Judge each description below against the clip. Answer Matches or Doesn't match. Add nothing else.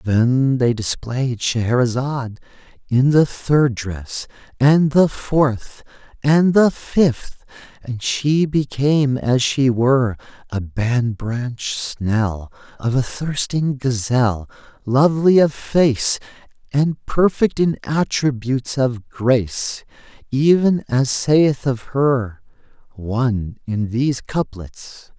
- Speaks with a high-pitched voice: Doesn't match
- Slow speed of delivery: Matches